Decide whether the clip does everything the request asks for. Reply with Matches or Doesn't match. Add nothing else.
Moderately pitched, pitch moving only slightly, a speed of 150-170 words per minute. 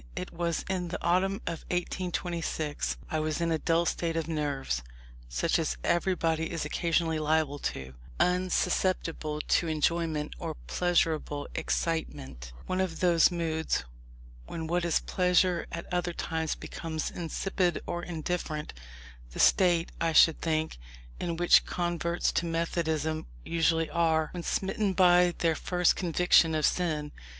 Doesn't match